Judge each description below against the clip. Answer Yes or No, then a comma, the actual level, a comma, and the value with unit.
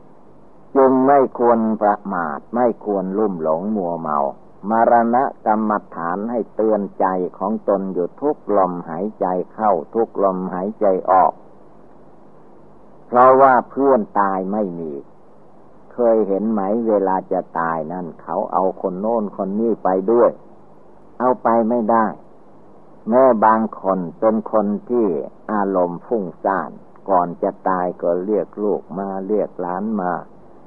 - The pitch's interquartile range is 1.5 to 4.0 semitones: Yes, average, 3.6 semitones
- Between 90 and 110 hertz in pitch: Yes, low, 105 Hz